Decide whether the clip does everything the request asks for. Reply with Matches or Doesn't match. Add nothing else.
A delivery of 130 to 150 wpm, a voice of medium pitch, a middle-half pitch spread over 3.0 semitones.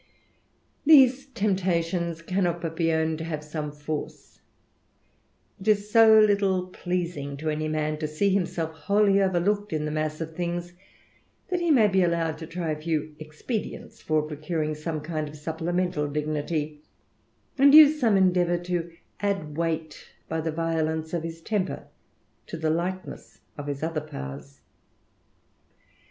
Matches